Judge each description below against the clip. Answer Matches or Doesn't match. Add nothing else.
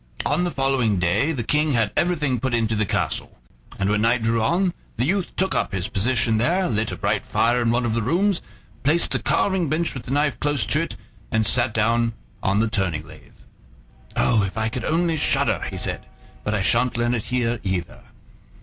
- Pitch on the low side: Matches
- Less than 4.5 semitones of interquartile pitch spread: Doesn't match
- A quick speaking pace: Matches